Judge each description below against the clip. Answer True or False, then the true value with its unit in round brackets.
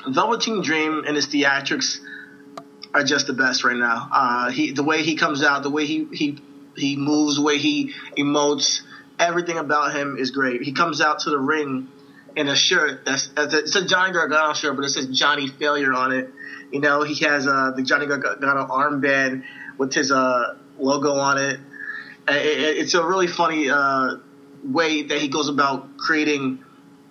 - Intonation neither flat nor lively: False (1.9 semitones)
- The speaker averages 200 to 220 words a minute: False (180 wpm)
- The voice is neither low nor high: True (145 Hz)